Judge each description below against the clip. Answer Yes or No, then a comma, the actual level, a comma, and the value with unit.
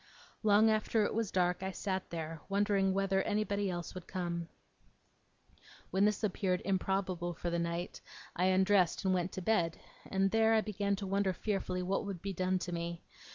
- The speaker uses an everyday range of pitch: No, narrow, 2.2 semitones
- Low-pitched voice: No, high, 190 Hz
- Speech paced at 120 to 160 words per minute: No, average, 180 wpm